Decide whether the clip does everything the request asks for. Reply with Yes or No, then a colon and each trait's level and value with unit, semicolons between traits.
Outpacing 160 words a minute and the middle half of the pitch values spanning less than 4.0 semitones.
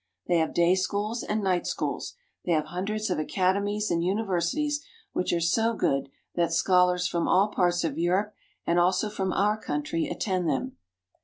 Yes: average, 170 wpm; average, 3.4 semitones